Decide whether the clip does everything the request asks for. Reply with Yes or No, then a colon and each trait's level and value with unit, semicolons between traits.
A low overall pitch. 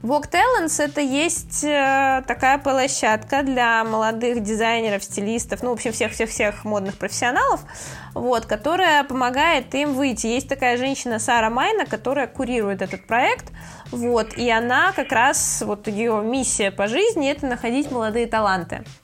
No: high, 240 Hz